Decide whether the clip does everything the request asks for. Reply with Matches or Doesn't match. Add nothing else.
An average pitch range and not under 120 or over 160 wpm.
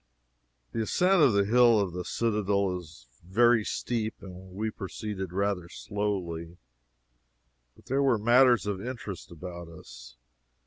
Matches